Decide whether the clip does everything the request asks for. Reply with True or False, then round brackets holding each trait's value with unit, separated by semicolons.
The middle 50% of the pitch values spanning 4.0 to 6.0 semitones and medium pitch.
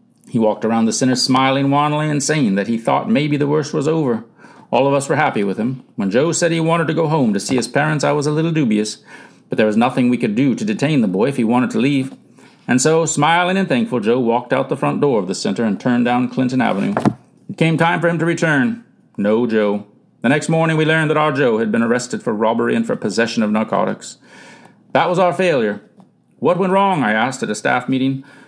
True (5.0 semitones; 150 Hz)